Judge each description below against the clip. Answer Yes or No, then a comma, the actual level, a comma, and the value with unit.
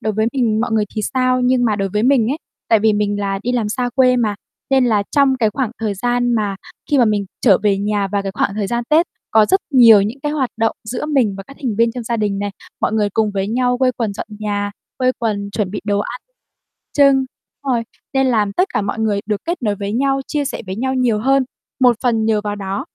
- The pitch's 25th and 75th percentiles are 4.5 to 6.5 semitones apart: No, average, 3.5 semitones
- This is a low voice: No, high, 225 Hz